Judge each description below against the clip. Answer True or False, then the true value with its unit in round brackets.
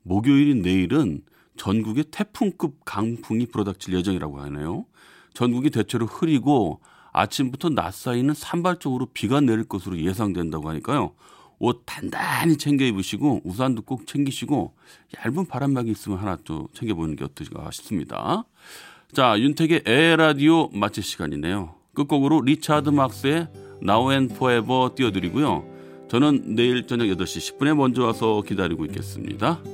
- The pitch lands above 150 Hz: False (120 Hz)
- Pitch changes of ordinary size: False (6.7 semitones)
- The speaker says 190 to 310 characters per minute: False (350 characters per minute)